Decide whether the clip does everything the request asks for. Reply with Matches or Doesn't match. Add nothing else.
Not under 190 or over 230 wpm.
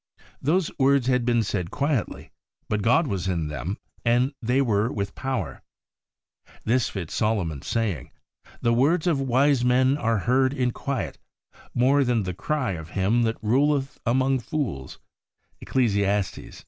Doesn't match